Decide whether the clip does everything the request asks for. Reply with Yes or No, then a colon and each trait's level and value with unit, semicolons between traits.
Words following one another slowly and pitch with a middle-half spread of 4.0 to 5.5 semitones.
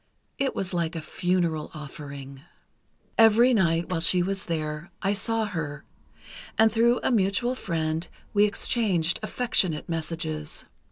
Yes: slow, 130 wpm; average, 4.9 semitones